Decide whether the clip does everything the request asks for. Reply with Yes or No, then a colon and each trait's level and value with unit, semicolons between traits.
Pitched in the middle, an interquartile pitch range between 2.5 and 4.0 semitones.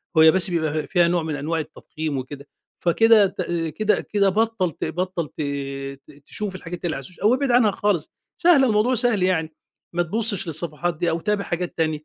No: medium, 175 Hz; average, 4.7 semitones